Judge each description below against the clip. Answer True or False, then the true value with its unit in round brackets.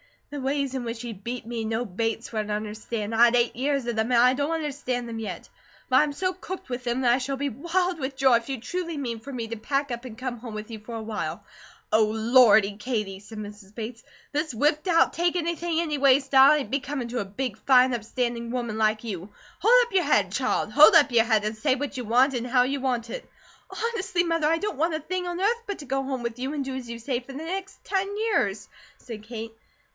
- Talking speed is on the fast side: True (245 wpm)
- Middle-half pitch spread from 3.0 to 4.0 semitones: False (4.5 semitones)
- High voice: True (255 Hz)